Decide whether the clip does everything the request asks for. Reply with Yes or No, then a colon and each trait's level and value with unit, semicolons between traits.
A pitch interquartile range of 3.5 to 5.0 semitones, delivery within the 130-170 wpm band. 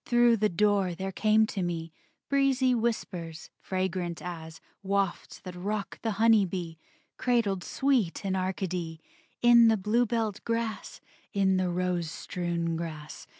Yes: average, 4.3 semitones; slow, 135 wpm